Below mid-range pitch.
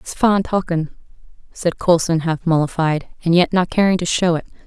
No: medium, 170 Hz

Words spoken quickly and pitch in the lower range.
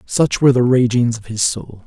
Yes: fast, 225 wpm; low, 120 Hz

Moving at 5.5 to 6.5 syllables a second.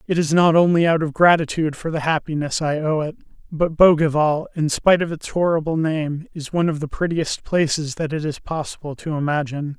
Yes: 5.7 syllables/s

